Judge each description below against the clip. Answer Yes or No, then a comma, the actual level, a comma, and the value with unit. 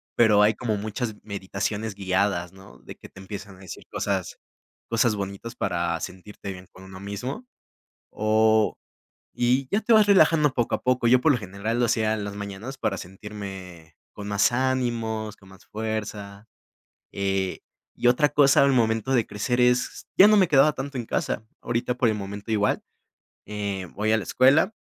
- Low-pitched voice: Yes, low, 110 Hz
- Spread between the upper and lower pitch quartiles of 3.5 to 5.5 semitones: Yes, average, 3.8 semitones